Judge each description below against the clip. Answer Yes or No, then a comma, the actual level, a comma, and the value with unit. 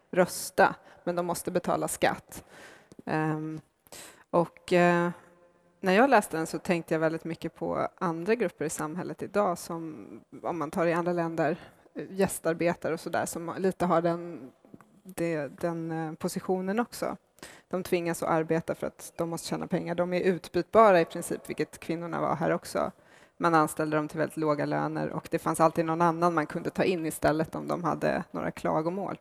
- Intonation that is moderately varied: No, narrow, 1.6 semitones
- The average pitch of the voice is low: No, medium, 170 Hz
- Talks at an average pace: Yes, average, 170 wpm